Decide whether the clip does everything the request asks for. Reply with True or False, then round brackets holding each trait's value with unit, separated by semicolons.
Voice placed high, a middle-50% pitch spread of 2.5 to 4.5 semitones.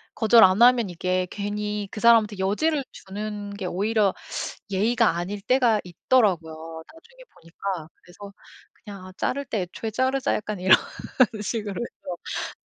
True (205 Hz; 3.7 semitones)